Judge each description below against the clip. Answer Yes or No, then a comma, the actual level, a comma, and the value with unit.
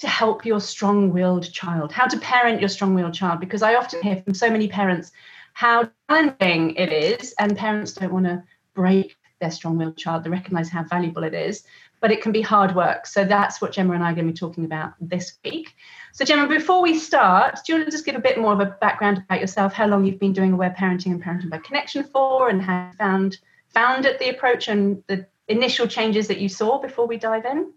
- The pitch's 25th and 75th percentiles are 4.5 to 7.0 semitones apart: Yes, average, 4.9 semitones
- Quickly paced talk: Yes, fast, 240 wpm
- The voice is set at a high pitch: Yes, high, 200 Hz